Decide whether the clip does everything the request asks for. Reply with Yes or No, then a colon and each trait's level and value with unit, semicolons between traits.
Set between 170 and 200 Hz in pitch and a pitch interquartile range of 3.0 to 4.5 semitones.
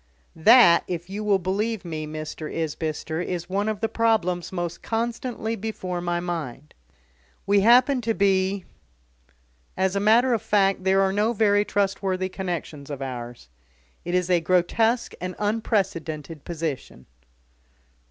Yes: high, 190 Hz; average, 3.9 semitones